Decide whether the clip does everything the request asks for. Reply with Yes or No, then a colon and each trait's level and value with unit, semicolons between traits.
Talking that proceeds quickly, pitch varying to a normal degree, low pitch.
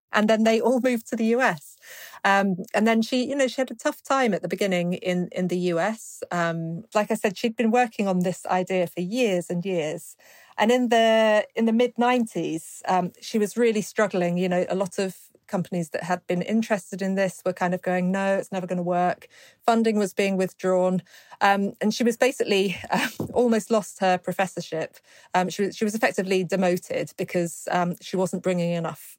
No: fast, 210 wpm; average, 3.8 semitones; high, 195 Hz